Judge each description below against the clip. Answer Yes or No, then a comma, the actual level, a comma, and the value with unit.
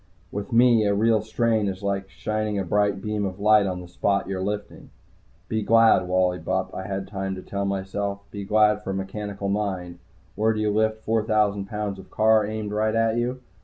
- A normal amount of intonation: No, narrow, 1.9 semitones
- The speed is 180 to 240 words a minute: Yes, fast, 205 wpm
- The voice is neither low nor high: No, low, 105 Hz